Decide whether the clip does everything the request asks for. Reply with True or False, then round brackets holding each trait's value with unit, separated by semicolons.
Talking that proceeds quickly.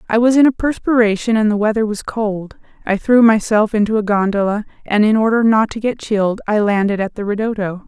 True (215 wpm)